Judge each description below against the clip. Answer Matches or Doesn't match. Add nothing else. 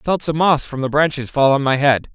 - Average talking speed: Doesn't match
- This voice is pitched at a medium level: Matches